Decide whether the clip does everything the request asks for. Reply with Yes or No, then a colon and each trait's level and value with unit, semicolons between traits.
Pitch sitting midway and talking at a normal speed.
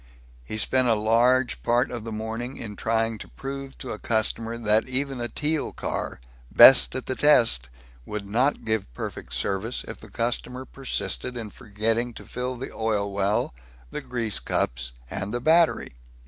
No: low, 115 Hz; average, 170 wpm